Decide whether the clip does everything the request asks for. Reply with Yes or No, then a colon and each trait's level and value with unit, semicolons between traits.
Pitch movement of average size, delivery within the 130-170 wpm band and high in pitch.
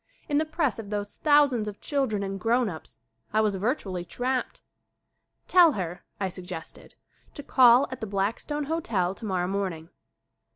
No: wide, 5.8 semitones; average, 160 wpm; high, 215 Hz